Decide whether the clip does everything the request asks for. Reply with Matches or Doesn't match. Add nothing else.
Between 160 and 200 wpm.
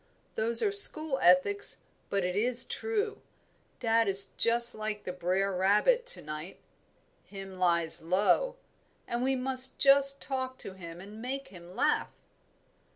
Doesn't match